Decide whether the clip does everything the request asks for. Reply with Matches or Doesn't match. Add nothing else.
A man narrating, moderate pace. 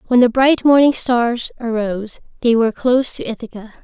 Doesn't match